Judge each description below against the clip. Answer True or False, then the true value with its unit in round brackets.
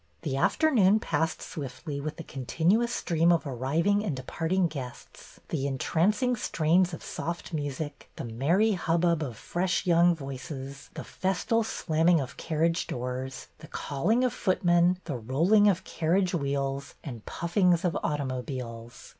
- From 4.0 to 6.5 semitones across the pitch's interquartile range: True (4.7 semitones)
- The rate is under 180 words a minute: True (145 wpm)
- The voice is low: False (160 Hz)